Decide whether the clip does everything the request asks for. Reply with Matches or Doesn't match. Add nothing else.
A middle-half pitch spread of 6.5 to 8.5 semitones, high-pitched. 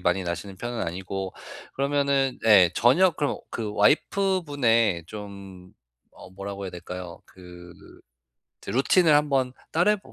Doesn't match